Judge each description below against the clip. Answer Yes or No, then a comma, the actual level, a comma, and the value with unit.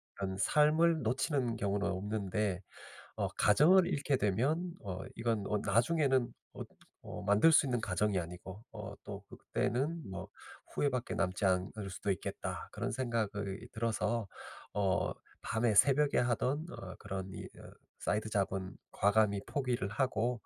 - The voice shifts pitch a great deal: No, average, 4.6 semitones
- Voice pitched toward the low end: Yes, low, 110 Hz